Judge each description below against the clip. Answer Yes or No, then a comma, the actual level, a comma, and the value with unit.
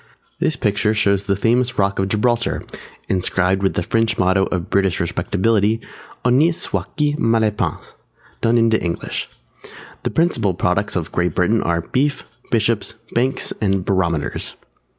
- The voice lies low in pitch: Yes, low, 105 Hz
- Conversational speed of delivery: Yes, average, 150 wpm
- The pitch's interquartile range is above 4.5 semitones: No, average, 3.5 semitones